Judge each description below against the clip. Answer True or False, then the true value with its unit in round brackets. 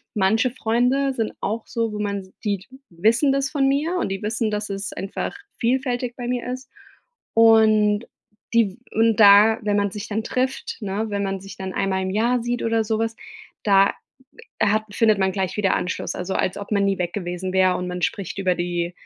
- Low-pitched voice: False (210 Hz)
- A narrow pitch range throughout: False (3.0 semitones)